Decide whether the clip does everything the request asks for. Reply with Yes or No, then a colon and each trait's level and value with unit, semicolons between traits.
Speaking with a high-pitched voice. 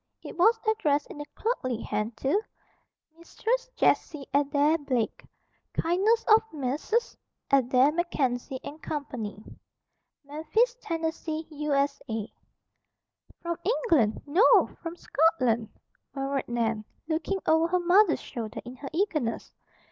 Yes: very high, 300 Hz